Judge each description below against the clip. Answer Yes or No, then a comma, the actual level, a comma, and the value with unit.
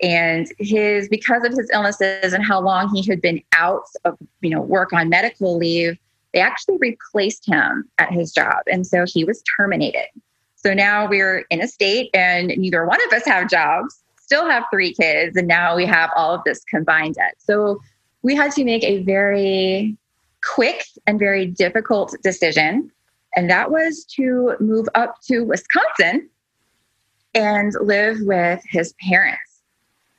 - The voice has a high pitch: Yes, high, 195 Hz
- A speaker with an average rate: Yes, average, 165 wpm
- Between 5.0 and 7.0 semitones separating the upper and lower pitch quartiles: No, average, 4.0 semitones